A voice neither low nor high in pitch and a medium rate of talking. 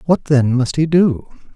Yes: medium, 145 Hz; average, 195 wpm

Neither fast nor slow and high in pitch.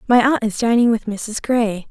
No: fast, 220 wpm; high, 225 Hz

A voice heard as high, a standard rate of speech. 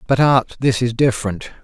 No: low, 125 Hz; average, 185 wpm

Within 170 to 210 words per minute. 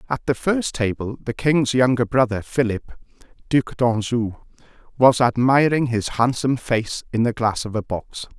No: average, 155 wpm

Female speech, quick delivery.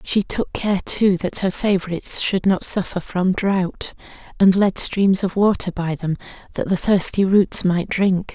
No: female; average, 180 wpm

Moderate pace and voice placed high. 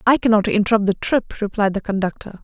Yes: average, 195 wpm; high, 210 Hz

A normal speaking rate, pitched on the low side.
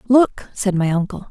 No: average, 185 wpm; high, 205 Hz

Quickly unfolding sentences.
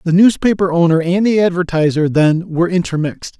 No: average, 160 wpm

